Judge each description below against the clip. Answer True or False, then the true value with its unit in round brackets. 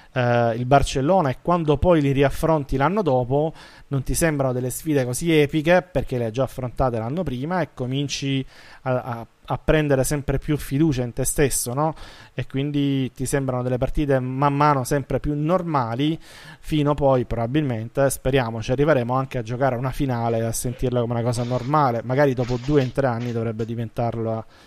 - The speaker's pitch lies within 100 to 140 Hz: True (135 Hz)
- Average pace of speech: False (180 wpm)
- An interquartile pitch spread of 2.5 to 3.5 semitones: True (2.8 semitones)